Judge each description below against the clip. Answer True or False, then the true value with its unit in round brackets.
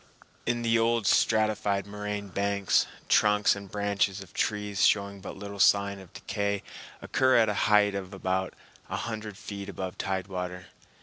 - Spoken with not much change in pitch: True (1.2 semitones)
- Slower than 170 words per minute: True (160 wpm)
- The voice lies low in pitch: True (100 Hz)